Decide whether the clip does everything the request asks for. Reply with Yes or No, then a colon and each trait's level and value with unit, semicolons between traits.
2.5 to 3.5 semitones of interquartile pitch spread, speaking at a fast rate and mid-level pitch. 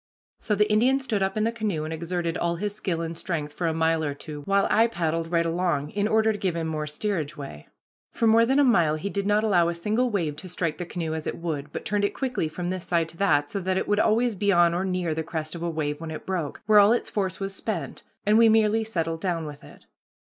No: average, 4.4 semitones; fast, 270 wpm; medium, 175 Hz